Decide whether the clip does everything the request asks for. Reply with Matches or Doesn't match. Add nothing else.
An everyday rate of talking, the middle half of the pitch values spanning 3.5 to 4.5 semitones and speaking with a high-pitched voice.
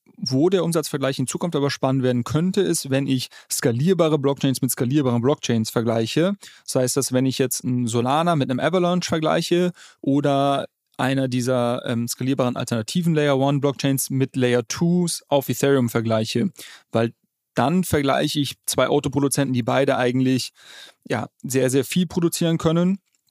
Doesn't match